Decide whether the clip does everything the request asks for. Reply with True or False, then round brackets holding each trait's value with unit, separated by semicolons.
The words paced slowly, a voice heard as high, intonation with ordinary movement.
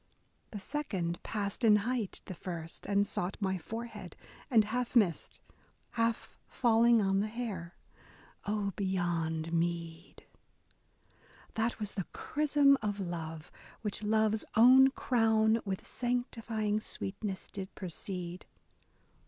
True (115 wpm; 210 Hz; 3.9 semitones)